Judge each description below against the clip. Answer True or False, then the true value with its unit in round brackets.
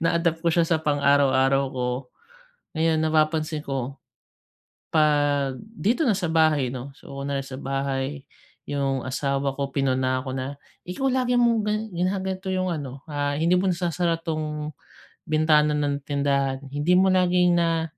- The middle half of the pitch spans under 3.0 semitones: False (3.6 semitones)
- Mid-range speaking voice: True (150 Hz)